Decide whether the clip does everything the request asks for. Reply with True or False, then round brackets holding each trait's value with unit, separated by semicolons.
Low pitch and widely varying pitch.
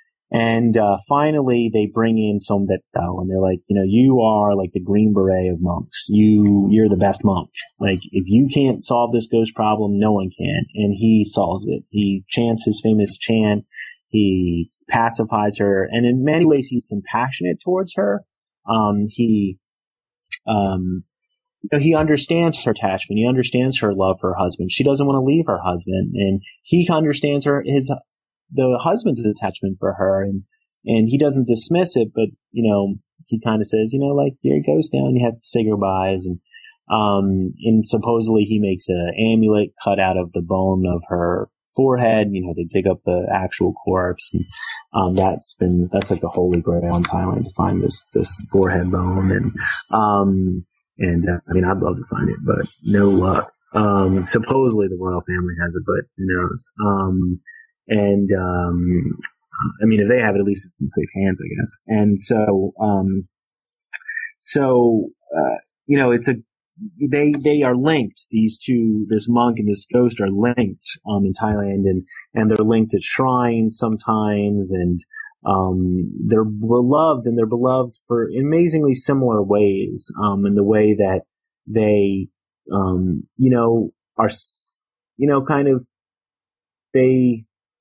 False (105 Hz; 4.1 semitones)